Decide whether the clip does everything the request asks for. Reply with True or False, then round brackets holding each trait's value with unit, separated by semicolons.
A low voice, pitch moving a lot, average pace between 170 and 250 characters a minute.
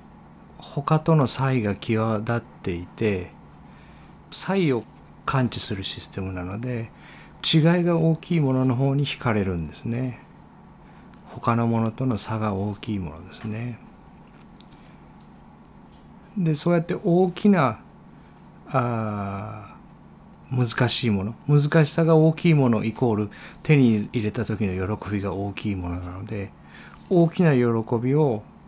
True (120 Hz; 6.9 semitones; 235 characters per minute)